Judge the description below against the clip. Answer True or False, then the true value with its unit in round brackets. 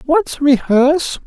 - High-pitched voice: True (260 Hz)